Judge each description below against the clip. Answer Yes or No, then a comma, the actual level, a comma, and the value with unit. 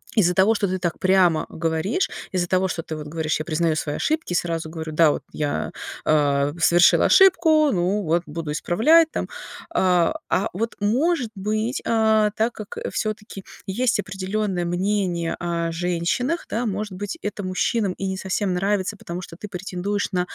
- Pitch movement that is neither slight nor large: Yes, average, 3.9 semitones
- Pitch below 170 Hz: No, medium, 185 Hz